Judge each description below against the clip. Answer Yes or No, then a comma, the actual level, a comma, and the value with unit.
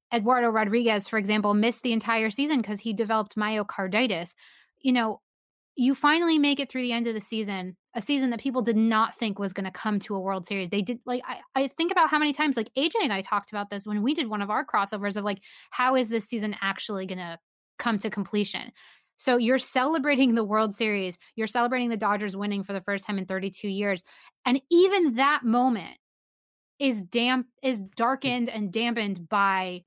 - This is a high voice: Yes, high, 225 Hz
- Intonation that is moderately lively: Yes, average, 3.8 semitones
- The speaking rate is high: Yes, fast, 210 wpm